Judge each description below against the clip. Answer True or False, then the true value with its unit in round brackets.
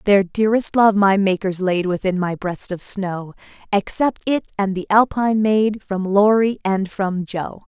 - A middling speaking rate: True (170 wpm)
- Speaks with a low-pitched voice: False (200 Hz)